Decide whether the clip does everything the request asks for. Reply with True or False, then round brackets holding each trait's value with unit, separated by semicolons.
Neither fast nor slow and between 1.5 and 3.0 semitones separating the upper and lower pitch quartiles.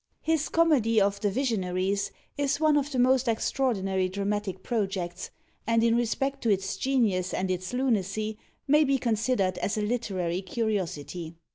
False (150 wpm; 5.1 semitones)